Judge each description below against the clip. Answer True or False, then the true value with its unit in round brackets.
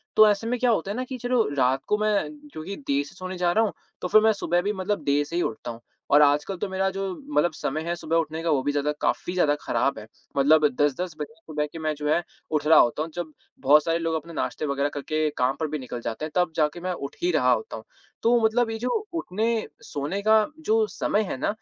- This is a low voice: False (170 Hz)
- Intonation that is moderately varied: False (6.1 semitones)